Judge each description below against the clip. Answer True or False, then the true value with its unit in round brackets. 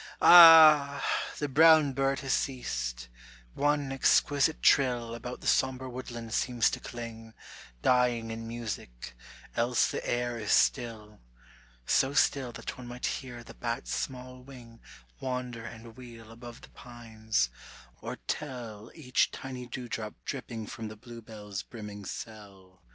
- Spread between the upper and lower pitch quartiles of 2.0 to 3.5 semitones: True (2.6 semitones)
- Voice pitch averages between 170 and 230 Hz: False (120 Hz)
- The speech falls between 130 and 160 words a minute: True (135 wpm)